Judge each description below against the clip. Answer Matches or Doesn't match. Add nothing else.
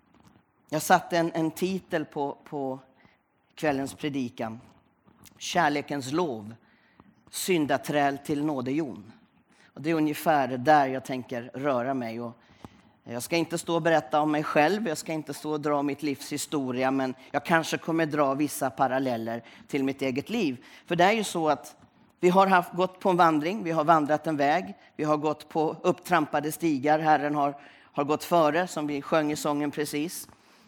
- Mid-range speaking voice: Matches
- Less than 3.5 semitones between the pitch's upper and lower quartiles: Matches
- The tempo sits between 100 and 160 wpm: Doesn't match